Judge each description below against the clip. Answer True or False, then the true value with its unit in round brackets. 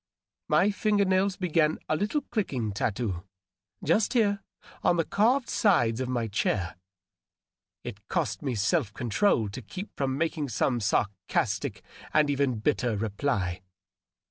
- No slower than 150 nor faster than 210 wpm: False (135 wpm)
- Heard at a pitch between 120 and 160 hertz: True (135 Hz)